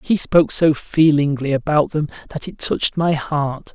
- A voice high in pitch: No, medium, 150 Hz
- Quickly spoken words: No, average, 175 wpm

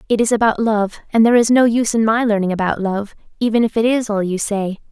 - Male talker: No, female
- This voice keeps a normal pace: No, fast, 255 wpm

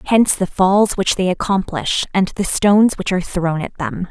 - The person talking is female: Yes, female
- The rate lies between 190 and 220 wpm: Yes, fast, 205 wpm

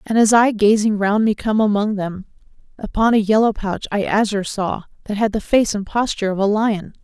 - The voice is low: No, high, 210 Hz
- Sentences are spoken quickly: Yes, fast, 215 wpm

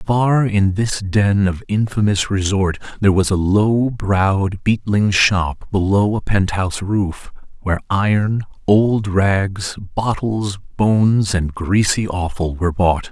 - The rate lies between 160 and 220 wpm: No, slow, 135 wpm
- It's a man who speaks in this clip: Yes, male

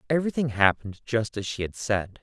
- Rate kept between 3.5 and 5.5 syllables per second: No, 6.0 syllables/s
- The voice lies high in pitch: No, low, 115 Hz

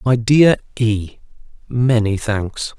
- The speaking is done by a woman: No, male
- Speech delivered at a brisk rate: No, slow, 85 wpm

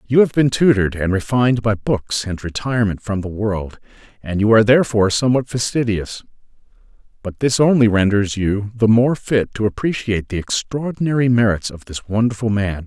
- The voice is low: Yes, low, 110 Hz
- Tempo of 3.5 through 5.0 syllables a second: No, 5.6 syllables/s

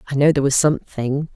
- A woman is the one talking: Yes, female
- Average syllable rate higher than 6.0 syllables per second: Yes, 7.3 syllables/s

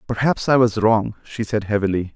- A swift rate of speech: No, average, 195 wpm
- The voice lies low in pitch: Yes, low, 110 Hz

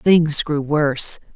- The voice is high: No, medium, 150 Hz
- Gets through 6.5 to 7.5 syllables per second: No, 3.4 syllables/s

